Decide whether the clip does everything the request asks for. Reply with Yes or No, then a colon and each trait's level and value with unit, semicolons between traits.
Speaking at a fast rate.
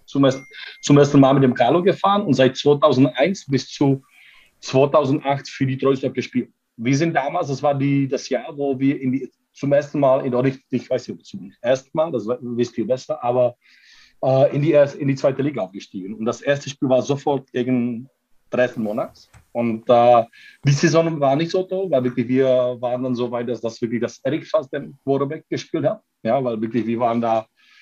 Yes: fast, 205 wpm